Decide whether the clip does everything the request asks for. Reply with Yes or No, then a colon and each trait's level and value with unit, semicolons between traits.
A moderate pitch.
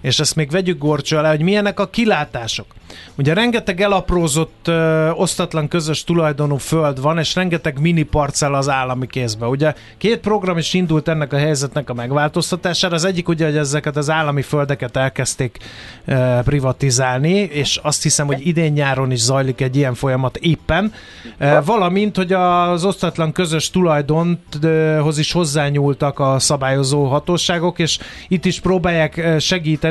Yes: medium, 155 Hz